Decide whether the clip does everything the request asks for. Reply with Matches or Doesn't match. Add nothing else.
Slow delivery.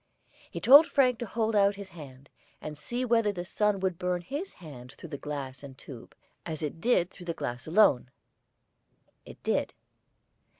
Doesn't match